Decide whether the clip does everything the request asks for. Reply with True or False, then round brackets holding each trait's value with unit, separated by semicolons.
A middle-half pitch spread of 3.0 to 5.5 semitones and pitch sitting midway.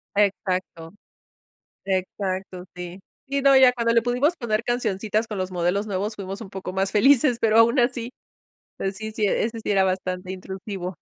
False (3.7 semitones; 205 Hz)